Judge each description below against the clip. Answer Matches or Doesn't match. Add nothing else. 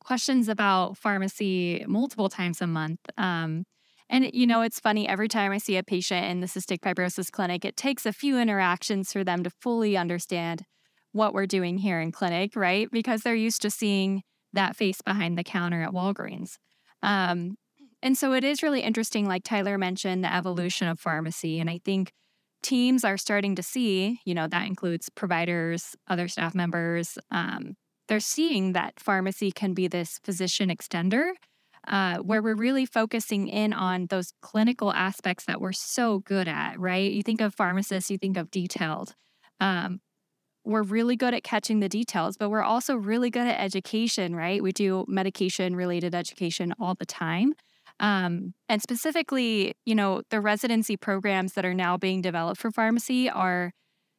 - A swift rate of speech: Doesn't match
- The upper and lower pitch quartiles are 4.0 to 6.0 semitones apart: Doesn't match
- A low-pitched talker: Doesn't match